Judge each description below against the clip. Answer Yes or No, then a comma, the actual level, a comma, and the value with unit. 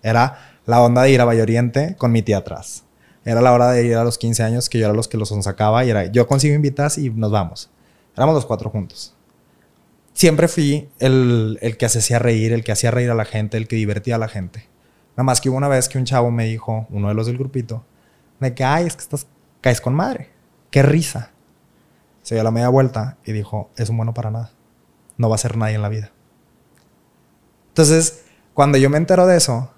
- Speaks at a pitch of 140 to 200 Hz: No, low, 120 Hz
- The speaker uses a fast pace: Yes, fast, 230 wpm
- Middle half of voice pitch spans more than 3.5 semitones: No, average, 3.2 semitones